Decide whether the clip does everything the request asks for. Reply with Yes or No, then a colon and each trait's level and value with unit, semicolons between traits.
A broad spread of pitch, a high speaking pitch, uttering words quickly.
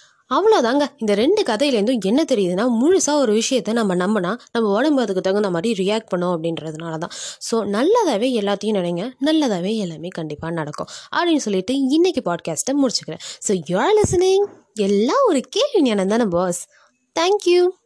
Yes: wide, 7.7 semitones; high, 230 Hz; fast, 145 wpm